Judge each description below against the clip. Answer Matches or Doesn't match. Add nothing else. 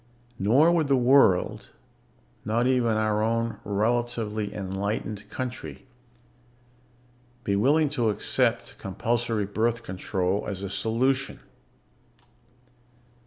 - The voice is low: Matches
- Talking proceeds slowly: Matches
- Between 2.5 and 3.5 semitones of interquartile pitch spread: Matches